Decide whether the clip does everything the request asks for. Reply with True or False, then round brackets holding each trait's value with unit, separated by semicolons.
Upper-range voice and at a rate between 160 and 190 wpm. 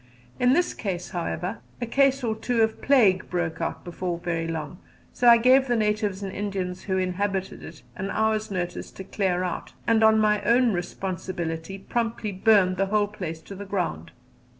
True (195 Hz; 175 wpm)